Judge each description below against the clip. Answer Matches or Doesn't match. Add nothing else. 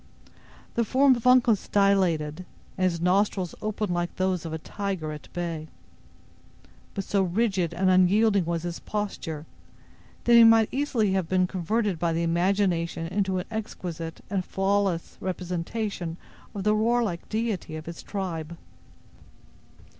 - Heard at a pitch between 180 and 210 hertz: Matches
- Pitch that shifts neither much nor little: Matches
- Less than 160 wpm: Matches